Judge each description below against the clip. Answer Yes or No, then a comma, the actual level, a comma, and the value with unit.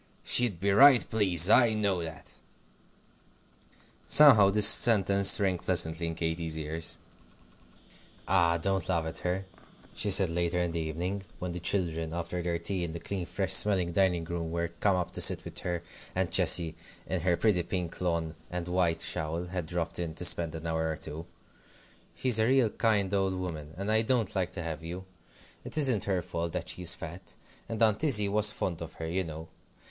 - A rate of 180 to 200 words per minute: Yes, average, 190 wpm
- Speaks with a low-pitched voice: Yes, very low, 90 Hz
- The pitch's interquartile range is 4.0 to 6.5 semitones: No, average, 3.1 semitones